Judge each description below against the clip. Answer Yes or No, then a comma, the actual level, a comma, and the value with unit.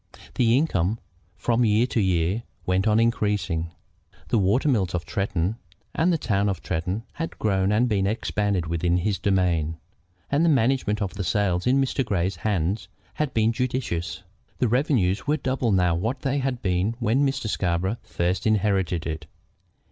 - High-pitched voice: No, low, 105 Hz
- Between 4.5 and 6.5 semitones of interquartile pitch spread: Yes, average, 4.9 semitones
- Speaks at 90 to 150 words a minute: No, average, 165 wpm